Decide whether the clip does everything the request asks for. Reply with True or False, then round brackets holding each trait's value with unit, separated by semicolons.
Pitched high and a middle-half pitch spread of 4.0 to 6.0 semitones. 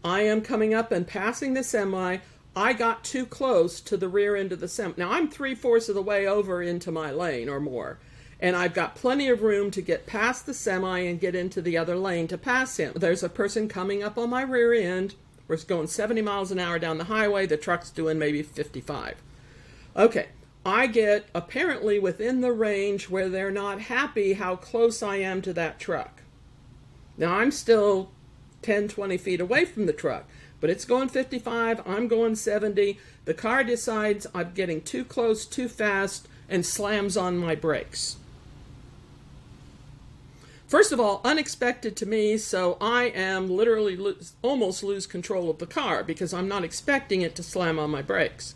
True (200 Hz; 4.3 semitones)